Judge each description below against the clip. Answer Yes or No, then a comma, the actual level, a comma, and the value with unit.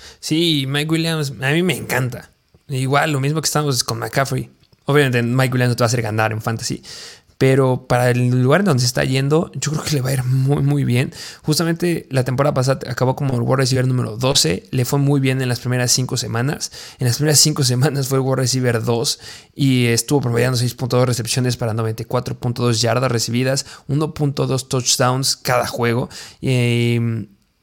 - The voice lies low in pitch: Yes, low, 130 Hz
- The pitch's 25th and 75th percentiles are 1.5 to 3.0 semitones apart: Yes, narrow, 2.6 semitones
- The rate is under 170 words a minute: No, fast, 190 wpm